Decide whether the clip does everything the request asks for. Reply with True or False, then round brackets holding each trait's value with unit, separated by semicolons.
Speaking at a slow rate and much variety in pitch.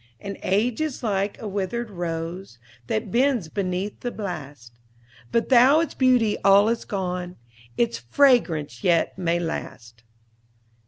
True (130 wpm; 5.9 semitones)